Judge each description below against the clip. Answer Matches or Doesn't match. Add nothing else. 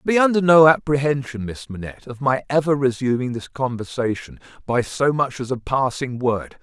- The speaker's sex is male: Matches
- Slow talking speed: Doesn't match